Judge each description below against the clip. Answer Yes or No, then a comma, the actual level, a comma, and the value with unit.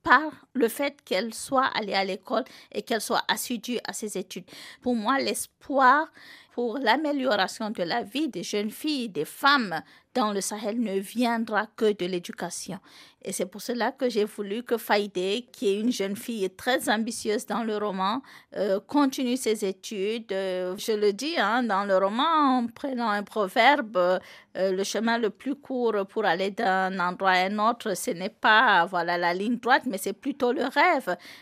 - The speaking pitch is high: Yes, high, 220 Hz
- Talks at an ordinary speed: Yes, average, 180 wpm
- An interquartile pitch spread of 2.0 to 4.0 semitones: No, average, 4.4 semitones